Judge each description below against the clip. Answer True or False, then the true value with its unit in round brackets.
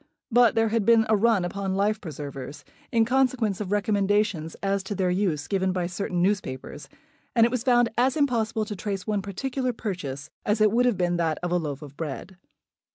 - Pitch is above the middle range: True (200 Hz)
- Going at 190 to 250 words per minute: True (195 wpm)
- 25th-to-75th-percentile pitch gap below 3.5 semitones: False (4.2 semitones)